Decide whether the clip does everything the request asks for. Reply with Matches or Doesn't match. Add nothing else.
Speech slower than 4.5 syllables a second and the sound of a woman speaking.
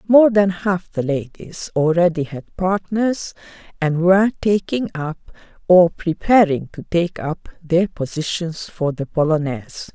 Matches